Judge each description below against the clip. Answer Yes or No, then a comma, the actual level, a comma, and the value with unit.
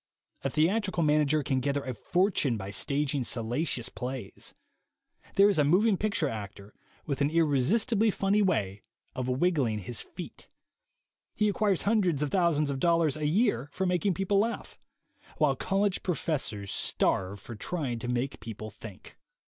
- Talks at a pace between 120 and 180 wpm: Yes, average, 155 wpm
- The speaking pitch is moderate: Yes, medium, 150 Hz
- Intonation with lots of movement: Yes, wide, 7.2 semitones